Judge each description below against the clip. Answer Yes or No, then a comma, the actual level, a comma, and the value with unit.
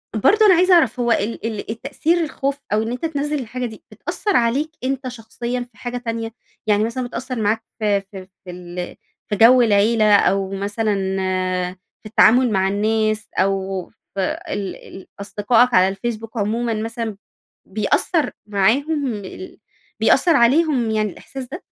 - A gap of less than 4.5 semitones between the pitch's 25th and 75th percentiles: Yes, average, 3.8 semitones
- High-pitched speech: Yes, high, 225 Hz